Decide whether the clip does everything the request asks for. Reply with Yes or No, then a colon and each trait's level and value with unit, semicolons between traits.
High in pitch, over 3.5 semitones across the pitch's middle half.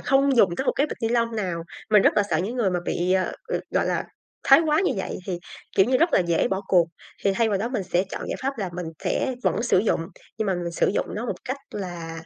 Yes: high, 200 Hz; wide, 5.4 semitones